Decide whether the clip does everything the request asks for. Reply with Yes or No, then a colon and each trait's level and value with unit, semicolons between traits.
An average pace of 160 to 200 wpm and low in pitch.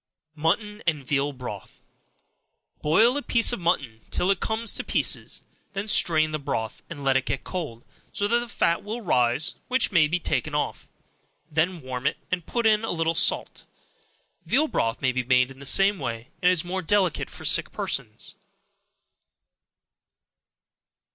No: average, 165 wpm; medium, 165 Hz